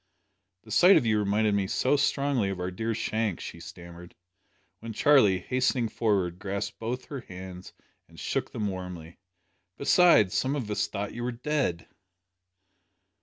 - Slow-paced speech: No, average, 155 wpm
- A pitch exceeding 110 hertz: No, low, 105 Hz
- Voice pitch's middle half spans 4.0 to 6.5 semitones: Yes, average, 5.1 semitones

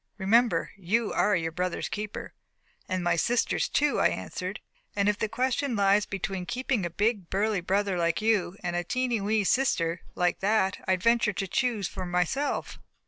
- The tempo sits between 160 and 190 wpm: Yes, average, 175 wpm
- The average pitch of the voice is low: No, high, 200 Hz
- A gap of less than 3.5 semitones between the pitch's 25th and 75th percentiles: No, average, 4.0 semitones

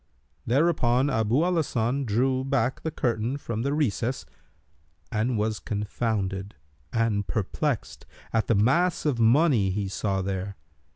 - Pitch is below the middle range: Yes, low, 115 Hz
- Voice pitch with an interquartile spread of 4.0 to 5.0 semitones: Yes, average, 4.5 semitones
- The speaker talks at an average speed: No, slow, 130 wpm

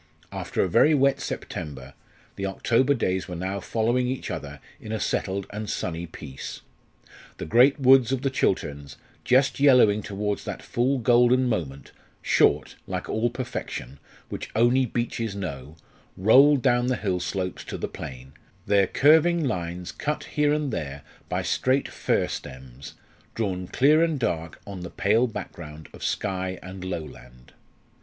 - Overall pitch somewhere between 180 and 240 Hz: No, low, 105 Hz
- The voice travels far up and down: Yes, wide, 6.6 semitones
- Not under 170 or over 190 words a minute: No, average, 150 wpm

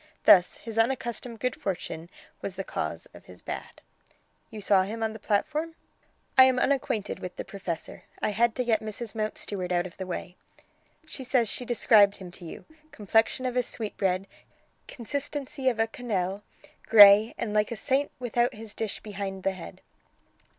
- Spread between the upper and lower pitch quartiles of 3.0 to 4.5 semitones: Yes, average, 3.9 semitones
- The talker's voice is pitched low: No, high, 220 Hz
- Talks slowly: No, average, 170 wpm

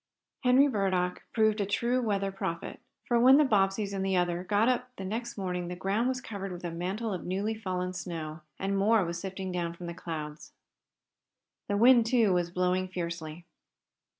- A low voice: No, high, 195 Hz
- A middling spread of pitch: Yes, average, 3.7 semitones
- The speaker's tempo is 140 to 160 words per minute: No, average, 185 wpm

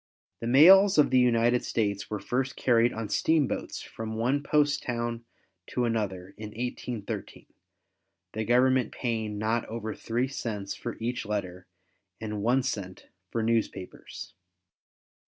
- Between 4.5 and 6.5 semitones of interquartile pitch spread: No, average, 2.7 semitones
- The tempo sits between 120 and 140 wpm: Yes, slow, 135 wpm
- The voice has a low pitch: Yes, low, 115 Hz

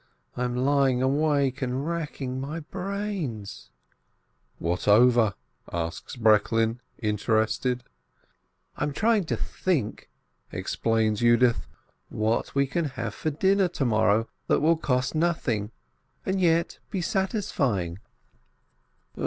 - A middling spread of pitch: No, wide, 6.2 semitones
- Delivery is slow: Yes, slow, 105 wpm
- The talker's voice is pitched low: Yes, low, 130 Hz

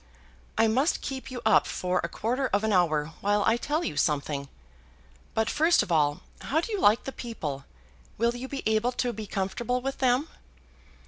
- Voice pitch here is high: Yes, high, 225 Hz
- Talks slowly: No, average, 190 wpm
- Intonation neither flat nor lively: No, wide, 6.2 semitones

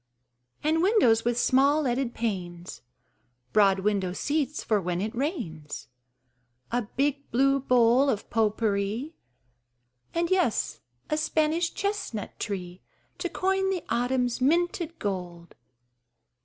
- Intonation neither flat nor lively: No, wide, 7.1 semitones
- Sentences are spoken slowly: Yes, slow, 115 wpm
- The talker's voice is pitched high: Yes, high, 245 Hz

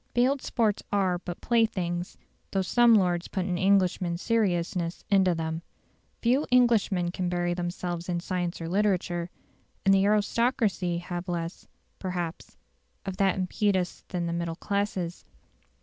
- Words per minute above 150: No, slow, 135 wpm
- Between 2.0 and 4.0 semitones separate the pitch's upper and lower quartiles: Yes, average, 2.7 semitones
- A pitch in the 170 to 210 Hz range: Yes, medium, 185 Hz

